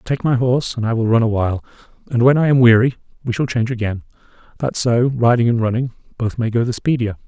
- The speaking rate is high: Yes, fast, 225 wpm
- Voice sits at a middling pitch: No, low, 120 Hz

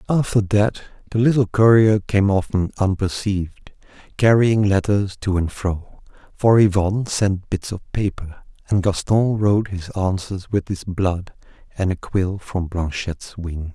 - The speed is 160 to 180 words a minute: No, average, 145 wpm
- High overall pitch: No, low, 100 Hz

